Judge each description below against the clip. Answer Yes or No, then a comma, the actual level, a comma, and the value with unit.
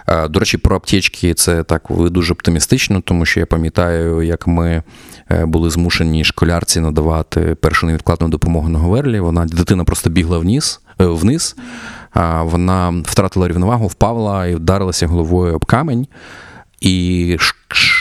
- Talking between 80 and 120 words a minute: No, average, 130 wpm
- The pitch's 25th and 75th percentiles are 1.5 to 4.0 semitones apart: Yes, average, 2.7 semitones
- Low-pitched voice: Yes, very low, 85 Hz